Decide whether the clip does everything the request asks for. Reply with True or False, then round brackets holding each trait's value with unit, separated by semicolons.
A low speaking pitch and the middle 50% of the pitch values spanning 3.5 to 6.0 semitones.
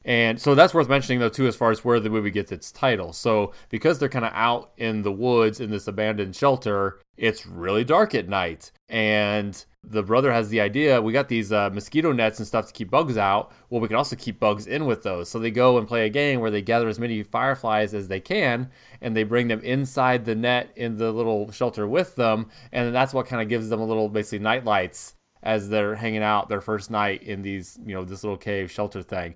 False (110 Hz; 2.5 semitones)